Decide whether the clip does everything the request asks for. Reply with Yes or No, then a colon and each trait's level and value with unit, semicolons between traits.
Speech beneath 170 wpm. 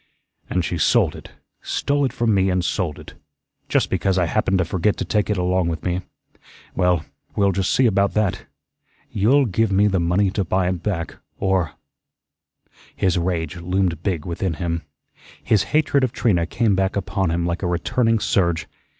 No: average, 185 wpm